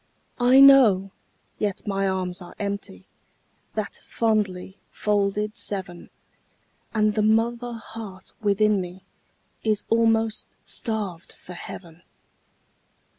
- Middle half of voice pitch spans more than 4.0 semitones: No, average, 2.8 semitones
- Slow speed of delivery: Yes, slow, 100 wpm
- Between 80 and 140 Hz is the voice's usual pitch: No, high, 210 Hz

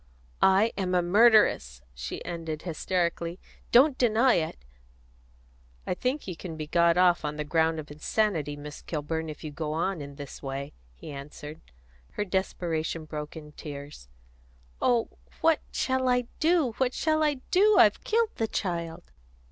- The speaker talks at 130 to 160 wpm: Yes, average, 155 wpm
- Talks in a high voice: No, medium, 170 Hz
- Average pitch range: No, wide, 6.8 semitones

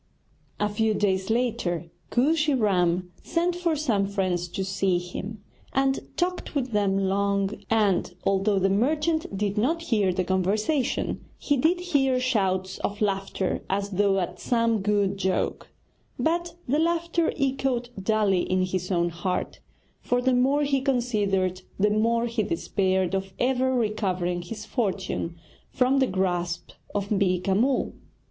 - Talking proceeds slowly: No, average, 145 wpm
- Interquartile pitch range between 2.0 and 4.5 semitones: No, average, 5.2 semitones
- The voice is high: Yes, high, 205 Hz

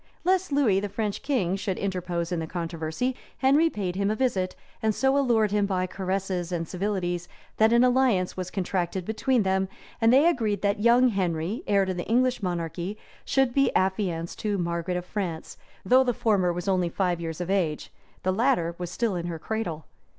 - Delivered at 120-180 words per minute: No, average, 190 wpm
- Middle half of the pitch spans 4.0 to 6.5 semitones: Yes, average, 4.4 semitones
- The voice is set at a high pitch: Yes, high, 195 Hz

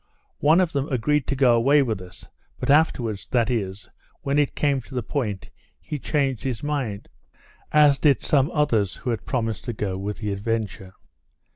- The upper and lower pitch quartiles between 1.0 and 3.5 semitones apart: No, average, 5.2 semitones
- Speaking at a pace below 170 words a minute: No, average, 180 wpm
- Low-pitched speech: Yes, low, 125 Hz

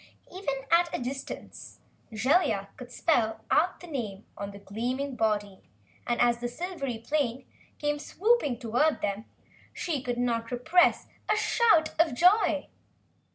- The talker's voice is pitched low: No, very high, 255 Hz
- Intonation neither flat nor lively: No, wide, 5.8 semitones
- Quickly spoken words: No, average, 140 wpm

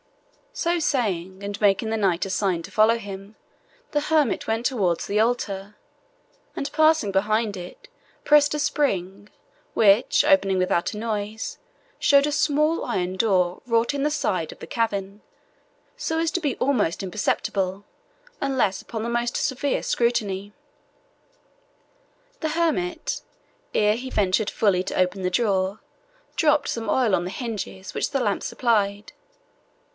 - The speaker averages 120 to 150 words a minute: Yes, average, 145 wpm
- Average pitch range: No, wide, 6.1 semitones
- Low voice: No, high, 215 Hz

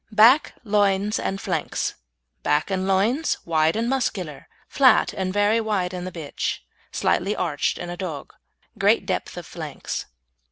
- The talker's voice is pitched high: Yes, high, 195 Hz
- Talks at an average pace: Yes, average, 150 wpm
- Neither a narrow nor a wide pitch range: Yes, average, 3.5 semitones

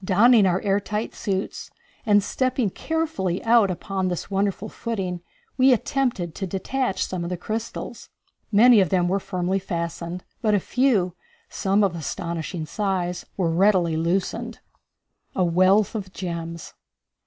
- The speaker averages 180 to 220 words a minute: No, average, 145 wpm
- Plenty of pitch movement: No, average, 3.2 semitones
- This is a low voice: No, high, 190 Hz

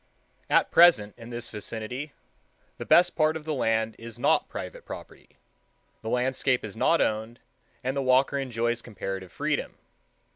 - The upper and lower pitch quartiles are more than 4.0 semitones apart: No, average, 3.7 semitones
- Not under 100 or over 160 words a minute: Yes, average, 150 wpm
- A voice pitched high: No, low, 120 Hz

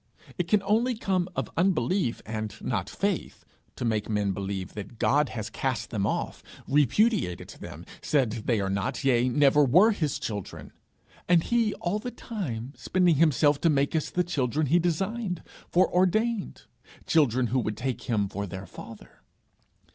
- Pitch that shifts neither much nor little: No, wide, 8.4 semitones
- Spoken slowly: No, average, 160 wpm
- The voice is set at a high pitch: No, medium, 140 Hz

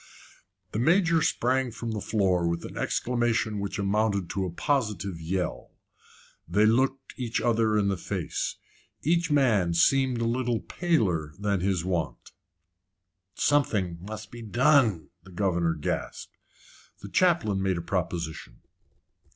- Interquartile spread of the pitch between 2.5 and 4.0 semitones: No, wide, 5.4 semitones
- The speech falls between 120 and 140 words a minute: Yes, slow, 135 wpm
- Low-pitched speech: Yes, low, 105 Hz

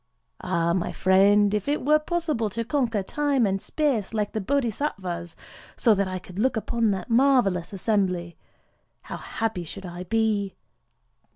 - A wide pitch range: No, average, 4.4 semitones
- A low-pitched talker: No, high, 210 Hz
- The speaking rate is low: No, average, 155 wpm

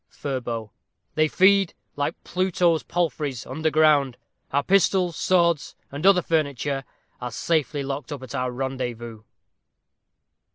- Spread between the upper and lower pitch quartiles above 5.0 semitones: No, average, 4.5 semitones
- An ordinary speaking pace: No, slow, 120 wpm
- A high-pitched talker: No, medium, 145 Hz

